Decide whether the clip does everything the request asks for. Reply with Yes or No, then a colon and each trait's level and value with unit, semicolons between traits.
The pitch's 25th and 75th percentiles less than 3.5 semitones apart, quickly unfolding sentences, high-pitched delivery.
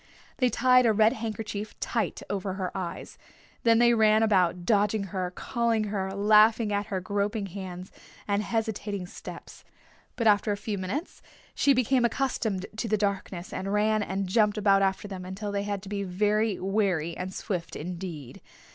No: narrow, 2.5 semitones; average, 170 wpm; high, 205 Hz